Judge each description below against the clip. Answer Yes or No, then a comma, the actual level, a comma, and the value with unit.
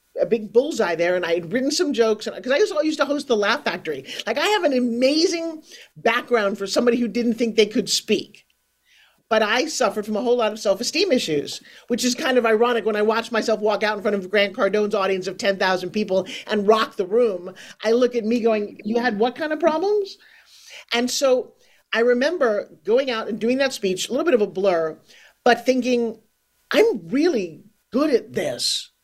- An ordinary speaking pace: No, fast, 210 wpm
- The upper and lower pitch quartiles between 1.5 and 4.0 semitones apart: No, average, 4.7 semitones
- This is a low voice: No, high, 235 Hz